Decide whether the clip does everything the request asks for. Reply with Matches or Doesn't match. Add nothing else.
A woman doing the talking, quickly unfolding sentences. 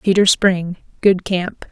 Doesn't match